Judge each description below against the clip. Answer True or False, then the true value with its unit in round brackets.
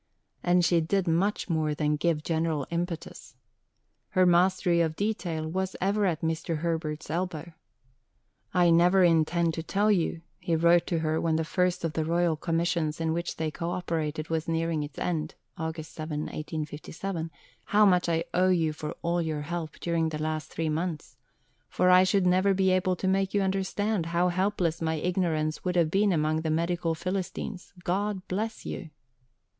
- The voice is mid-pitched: True (170 Hz)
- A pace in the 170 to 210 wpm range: True (175 wpm)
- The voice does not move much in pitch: True (2.3 semitones)